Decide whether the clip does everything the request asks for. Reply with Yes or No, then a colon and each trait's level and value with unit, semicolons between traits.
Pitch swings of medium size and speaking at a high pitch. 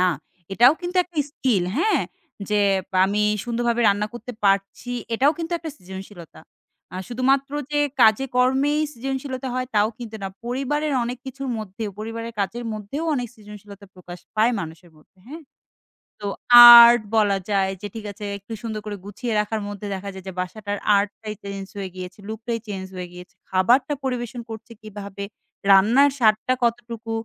Yes: average, 3.9 semitones; high, 220 Hz